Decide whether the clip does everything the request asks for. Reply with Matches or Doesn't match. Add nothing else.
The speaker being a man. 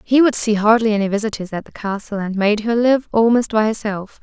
Doesn't match